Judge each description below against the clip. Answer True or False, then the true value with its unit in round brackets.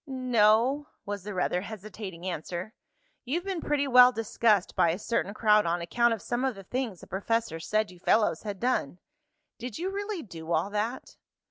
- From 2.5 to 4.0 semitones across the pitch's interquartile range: False (5.1 semitones)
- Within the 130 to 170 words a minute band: False (180 wpm)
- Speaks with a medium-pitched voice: False (215 Hz)